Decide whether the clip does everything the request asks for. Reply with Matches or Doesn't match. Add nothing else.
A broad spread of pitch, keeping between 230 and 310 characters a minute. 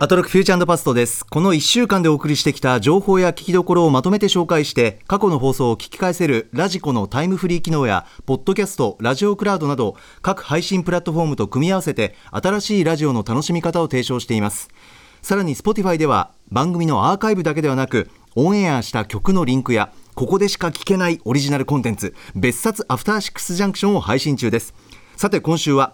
Doesn't match